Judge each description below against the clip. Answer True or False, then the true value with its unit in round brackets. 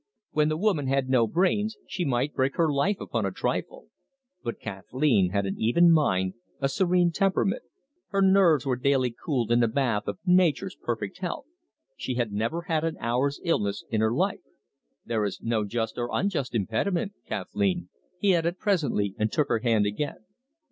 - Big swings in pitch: True (7.4 semitones)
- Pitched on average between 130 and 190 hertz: True (140 Hz)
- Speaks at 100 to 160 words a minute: False (175 wpm)